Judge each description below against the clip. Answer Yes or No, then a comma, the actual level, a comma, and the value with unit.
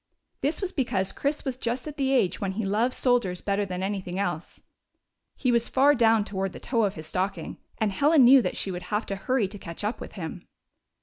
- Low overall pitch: No, high, 215 Hz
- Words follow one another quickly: Yes, fast, 225 wpm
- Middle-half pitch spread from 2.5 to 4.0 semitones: No, average, 5.0 semitones